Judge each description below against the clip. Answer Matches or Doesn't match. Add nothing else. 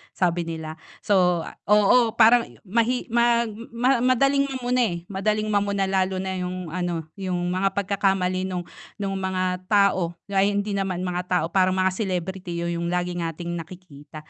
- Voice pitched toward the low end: Doesn't match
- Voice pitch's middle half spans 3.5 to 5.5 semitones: Doesn't match